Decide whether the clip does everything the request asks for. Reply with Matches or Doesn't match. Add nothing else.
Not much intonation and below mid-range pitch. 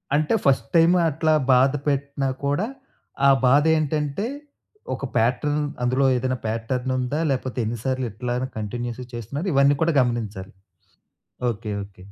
Doesn't match